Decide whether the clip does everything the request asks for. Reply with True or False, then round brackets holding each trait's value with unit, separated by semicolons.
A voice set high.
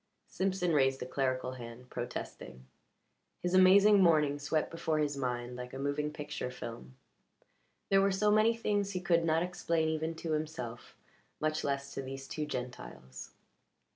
False (150 Hz)